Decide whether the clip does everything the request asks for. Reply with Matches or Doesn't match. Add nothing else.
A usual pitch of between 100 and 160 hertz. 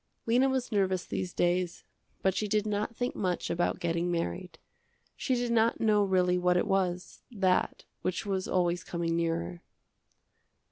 Doesn't match